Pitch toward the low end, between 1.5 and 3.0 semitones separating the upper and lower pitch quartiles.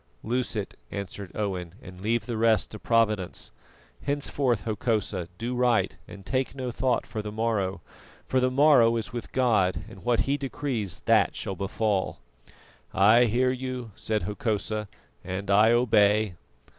No: low, 110 Hz; average, 3.5 semitones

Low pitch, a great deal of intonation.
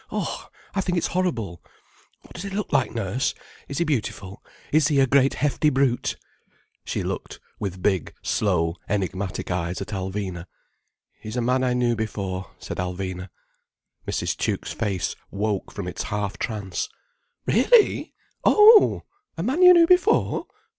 Yes: low, 110 Hz; wide, 8.4 semitones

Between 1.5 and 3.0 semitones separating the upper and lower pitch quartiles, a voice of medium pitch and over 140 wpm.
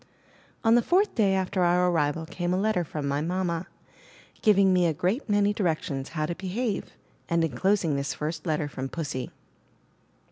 No: average, 3.9 semitones; medium, 175 Hz; average, 175 wpm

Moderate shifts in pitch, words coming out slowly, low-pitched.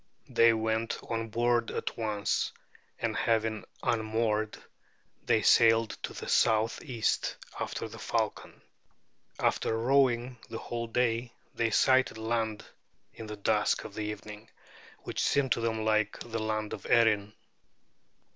No: narrow, 1.3 semitones; slow, 130 wpm; low, 115 Hz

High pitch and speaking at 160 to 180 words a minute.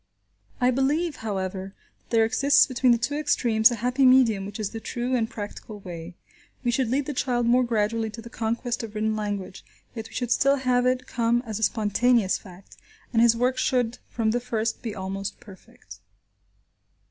No: high, 230 Hz; average, 190 wpm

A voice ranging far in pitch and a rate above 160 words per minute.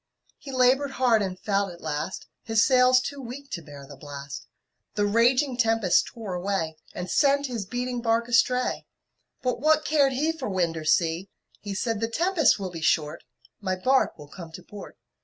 Yes: wide, 6.1 semitones; average, 185 wpm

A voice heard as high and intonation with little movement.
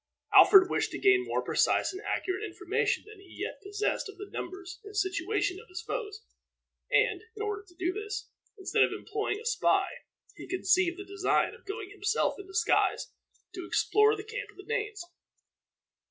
Yes: very high, 405 Hz; narrow, 2.1 semitones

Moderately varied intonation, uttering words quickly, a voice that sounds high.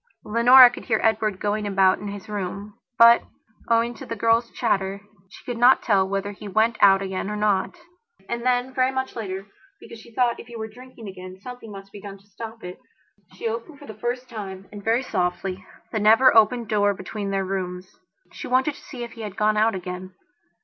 Yes: average, 3.2 semitones; fast, 210 wpm; high, 215 Hz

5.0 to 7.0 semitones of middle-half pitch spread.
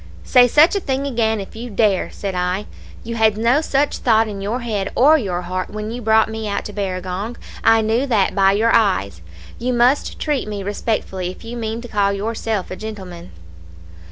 No: average, 3.2 semitones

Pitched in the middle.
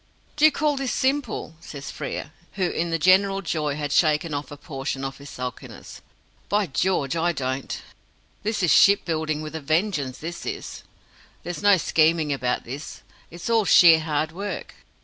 Yes: medium, 160 Hz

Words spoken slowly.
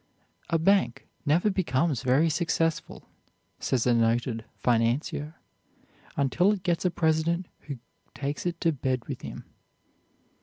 Yes: slow, 125 wpm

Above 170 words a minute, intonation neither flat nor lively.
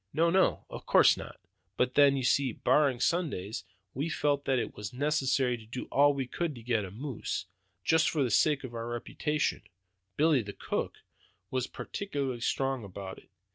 Yes: average, 180 wpm; average, 3.8 semitones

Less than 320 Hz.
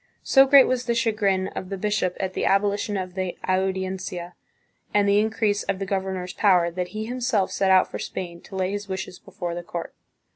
Yes: high, 190 Hz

